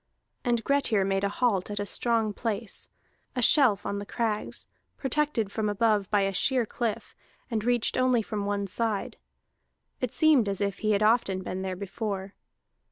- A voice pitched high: Yes, high, 215 Hz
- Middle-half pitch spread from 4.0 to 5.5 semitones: No, average, 3.0 semitones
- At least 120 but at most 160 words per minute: No, average, 170 wpm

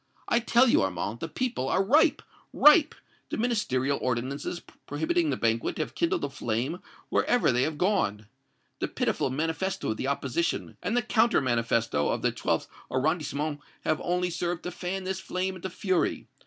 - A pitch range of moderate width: No, wide, 6.7 semitones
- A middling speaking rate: Yes, average, 170 wpm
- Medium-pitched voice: Yes, medium, 165 Hz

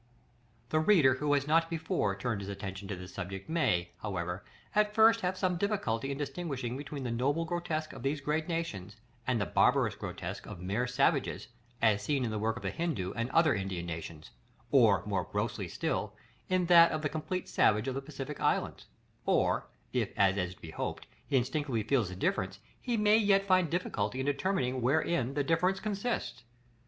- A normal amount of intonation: No, wide, 8.0 semitones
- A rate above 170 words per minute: Yes, average, 195 wpm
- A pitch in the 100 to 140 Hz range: Yes, low, 135 Hz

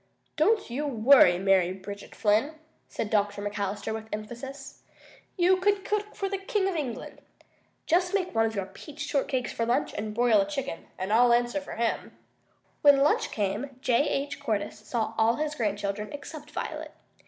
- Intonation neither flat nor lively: No, wide, 6.0 semitones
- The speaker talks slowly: No, average, 175 wpm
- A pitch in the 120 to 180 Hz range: No, high, 240 Hz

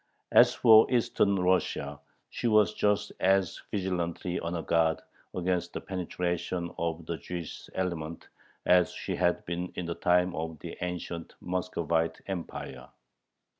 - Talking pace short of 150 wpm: Yes, slow, 135 wpm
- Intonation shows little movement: Yes, narrow, 1.8 semitones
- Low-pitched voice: Yes, very low, 90 Hz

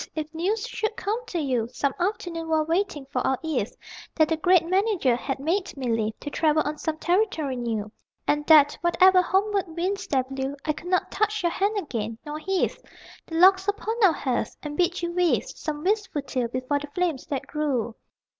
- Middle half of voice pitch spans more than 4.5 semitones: Yes, average, 5.2 semitones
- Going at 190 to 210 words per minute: Yes, average, 195 wpm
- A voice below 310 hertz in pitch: No, very high, 320 Hz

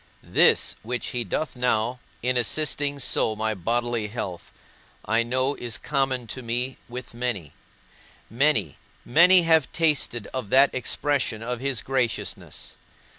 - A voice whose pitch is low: Yes, low, 125 Hz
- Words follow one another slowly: Yes, slow, 130 wpm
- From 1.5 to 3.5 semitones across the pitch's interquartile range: Yes, average, 3.0 semitones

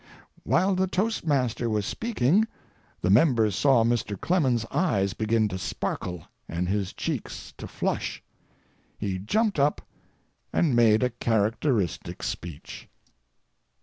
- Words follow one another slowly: Yes, slow, 115 wpm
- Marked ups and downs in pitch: Yes, wide, 6.7 semitones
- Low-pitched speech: Yes, low, 115 Hz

